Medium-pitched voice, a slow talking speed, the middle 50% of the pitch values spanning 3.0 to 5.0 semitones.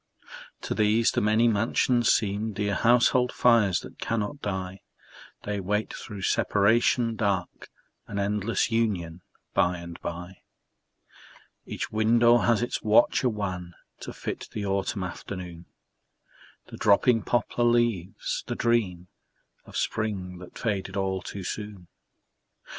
No: low, 105 Hz; slow, 125 wpm; average, 3.6 semitones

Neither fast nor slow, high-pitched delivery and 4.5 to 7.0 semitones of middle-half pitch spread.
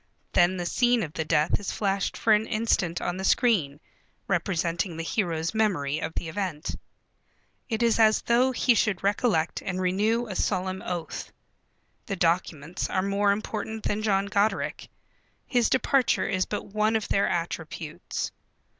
No: average, 155 wpm; high, 195 Hz; average, 4.0 semitones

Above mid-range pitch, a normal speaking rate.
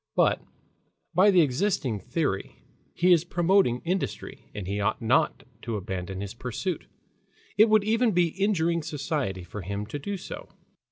No: medium, 155 Hz; average, 155 wpm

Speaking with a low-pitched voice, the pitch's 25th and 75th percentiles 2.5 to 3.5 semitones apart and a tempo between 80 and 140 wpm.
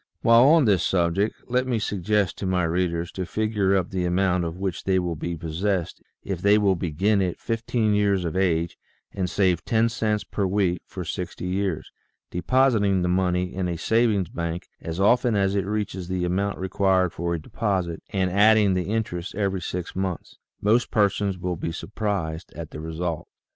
No: very low, 95 Hz; average, 2.8 semitones; average, 185 wpm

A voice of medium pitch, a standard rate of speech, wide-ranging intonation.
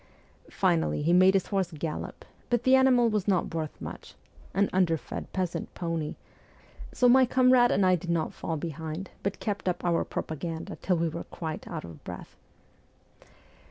No: medium, 180 Hz; average, 165 wpm; average, 3.9 semitones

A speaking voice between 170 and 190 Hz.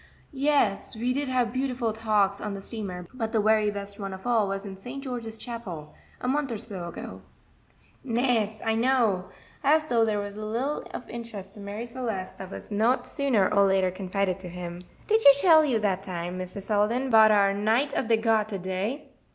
No: high, 215 Hz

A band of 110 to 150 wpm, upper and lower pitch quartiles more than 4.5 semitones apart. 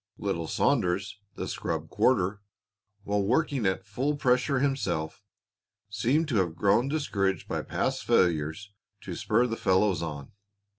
Yes: slow, 135 wpm; wide, 5.5 semitones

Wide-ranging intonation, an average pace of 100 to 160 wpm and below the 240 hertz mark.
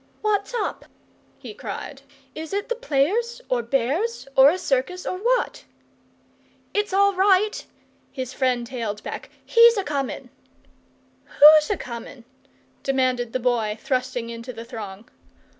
No: wide, 8.7 semitones; slow, 135 wpm; very high, 275 Hz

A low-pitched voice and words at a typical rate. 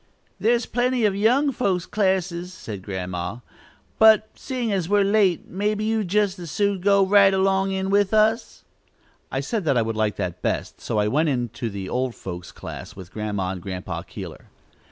No: high, 190 Hz; average, 180 wpm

